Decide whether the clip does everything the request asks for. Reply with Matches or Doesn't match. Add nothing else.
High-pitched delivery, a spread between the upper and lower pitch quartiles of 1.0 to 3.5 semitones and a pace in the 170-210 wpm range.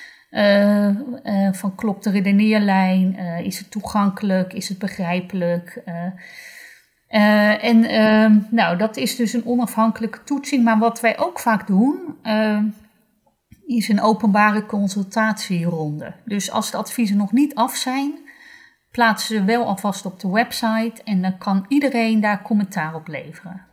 Doesn't match